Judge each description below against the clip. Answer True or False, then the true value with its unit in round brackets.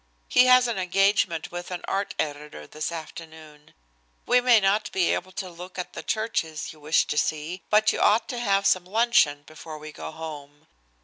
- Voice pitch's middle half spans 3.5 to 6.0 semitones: True (4.9 semitones)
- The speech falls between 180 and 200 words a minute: True (190 wpm)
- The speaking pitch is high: False (175 Hz)